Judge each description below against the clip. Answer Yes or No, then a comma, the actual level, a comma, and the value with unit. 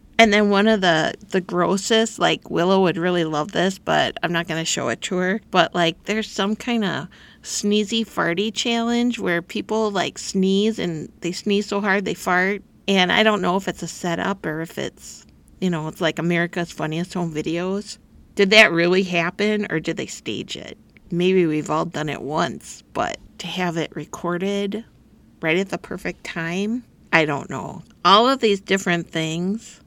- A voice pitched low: No, medium, 185 Hz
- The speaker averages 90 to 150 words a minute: No, average, 190 wpm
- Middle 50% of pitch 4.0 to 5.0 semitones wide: No, average, 3.4 semitones